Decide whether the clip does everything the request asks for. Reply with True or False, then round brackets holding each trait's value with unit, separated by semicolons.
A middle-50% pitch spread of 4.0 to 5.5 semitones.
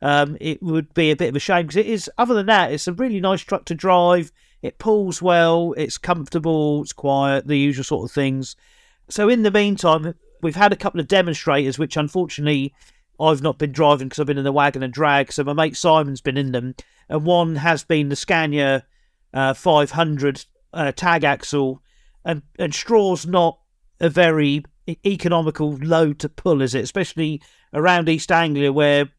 False (3.4 semitones)